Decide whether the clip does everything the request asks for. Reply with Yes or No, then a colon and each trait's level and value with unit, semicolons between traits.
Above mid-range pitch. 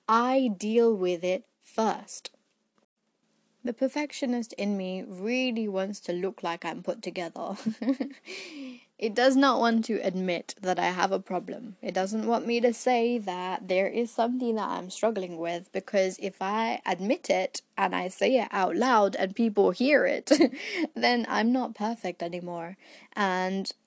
Yes: high, 220 Hz